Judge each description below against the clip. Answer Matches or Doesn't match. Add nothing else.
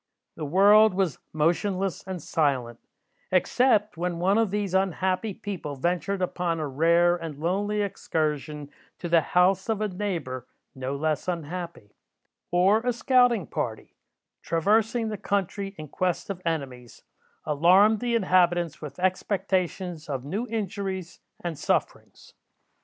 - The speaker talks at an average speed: Doesn't match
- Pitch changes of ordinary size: Matches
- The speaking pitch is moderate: Matches